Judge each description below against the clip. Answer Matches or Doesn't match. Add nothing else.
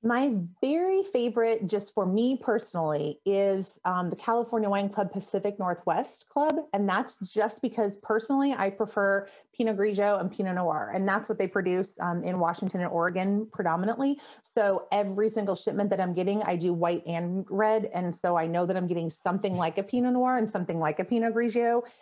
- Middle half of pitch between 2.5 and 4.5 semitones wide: Matches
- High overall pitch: Matches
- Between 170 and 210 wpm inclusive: Matches